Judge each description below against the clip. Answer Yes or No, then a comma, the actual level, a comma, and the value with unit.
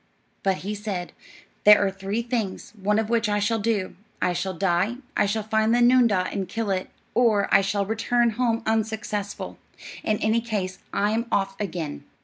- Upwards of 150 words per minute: Yes, average, 175 wpm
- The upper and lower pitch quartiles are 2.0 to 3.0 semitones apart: Yes, narrow, 2.6 semitones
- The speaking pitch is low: No, high, 210 Hz